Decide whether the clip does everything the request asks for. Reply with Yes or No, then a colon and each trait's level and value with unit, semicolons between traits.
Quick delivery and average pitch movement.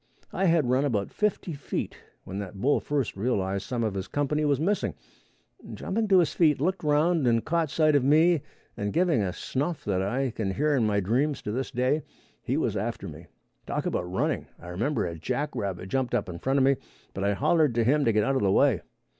No: fast, 220 wpm; wide, 6.8 semitones